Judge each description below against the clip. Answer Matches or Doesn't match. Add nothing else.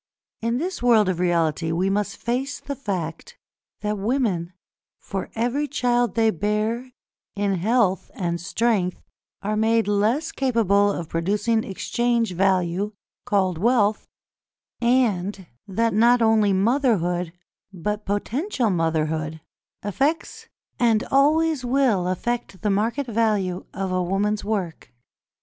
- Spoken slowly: Matches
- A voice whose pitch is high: Matches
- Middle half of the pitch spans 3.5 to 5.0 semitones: Matches